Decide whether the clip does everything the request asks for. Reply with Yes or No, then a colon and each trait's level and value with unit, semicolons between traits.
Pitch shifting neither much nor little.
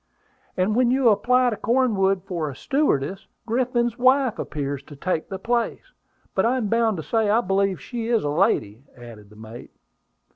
No: wide, 7.4 semitones